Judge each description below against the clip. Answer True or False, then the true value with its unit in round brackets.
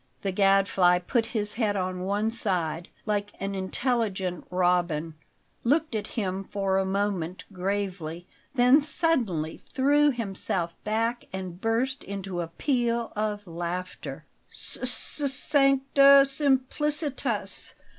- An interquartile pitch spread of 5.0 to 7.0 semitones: True (5.4 semitones)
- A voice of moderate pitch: False (205 Hz)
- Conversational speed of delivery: False (115 wpm)